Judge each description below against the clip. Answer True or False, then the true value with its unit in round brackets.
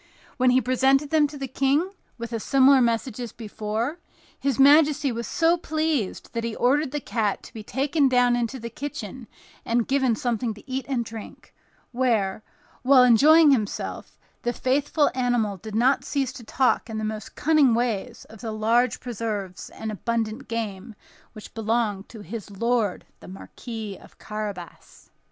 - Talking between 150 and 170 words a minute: True (165 wpm)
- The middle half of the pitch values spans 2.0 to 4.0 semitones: True (3.7 semitones)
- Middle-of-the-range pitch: False (240 Hz)